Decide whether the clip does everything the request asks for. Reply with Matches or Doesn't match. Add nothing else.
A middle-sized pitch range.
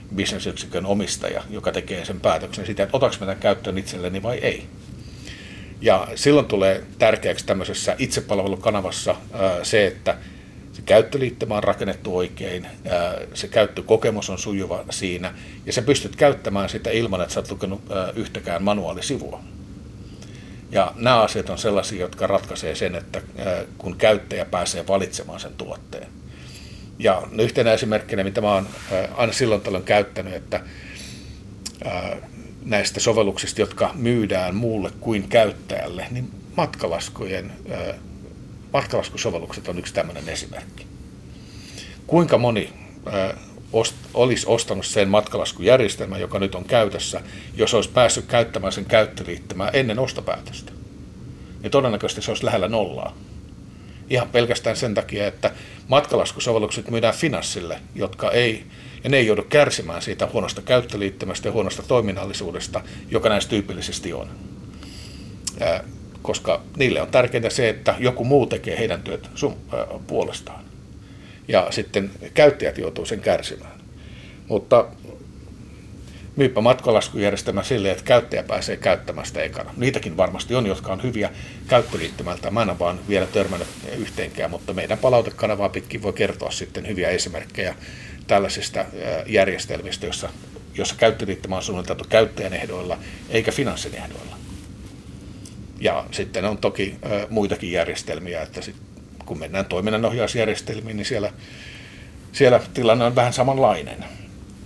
Matches